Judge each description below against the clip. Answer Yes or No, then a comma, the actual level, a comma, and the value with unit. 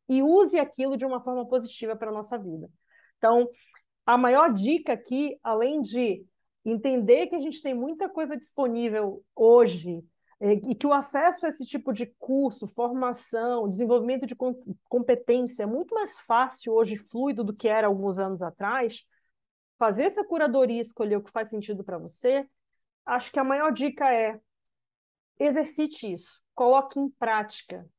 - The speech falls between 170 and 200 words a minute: No, average, 155 wpm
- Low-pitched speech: No, high, 245 Hz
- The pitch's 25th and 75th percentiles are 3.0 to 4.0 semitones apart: Yes, average, 3.6 semitones